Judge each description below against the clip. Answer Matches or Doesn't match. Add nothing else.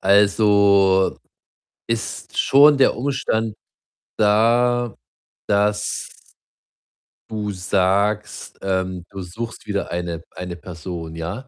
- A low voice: Matches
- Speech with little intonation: Doesn't match